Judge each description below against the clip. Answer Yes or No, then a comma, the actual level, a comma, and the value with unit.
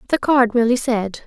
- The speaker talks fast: No, average, 190 wpm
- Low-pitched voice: No, high, 240 Hz